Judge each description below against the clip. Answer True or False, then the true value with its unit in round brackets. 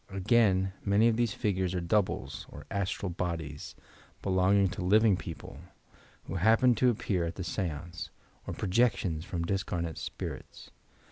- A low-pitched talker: True (95 Hz)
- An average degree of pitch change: True (3.3 semitones)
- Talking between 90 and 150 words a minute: True (145 wpm)